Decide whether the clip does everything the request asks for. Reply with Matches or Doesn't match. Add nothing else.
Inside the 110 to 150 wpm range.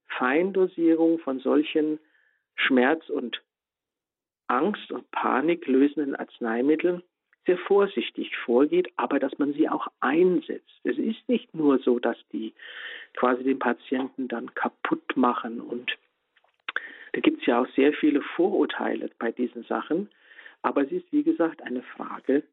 Matches